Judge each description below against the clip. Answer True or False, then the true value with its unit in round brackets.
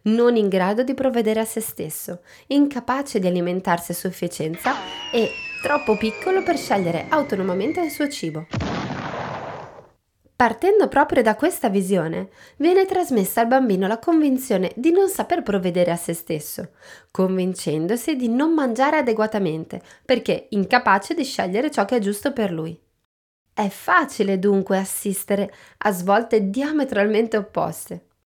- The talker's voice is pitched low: False (220 Hz)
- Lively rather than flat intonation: True (6.3 semitones)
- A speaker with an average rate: True (135 wpm)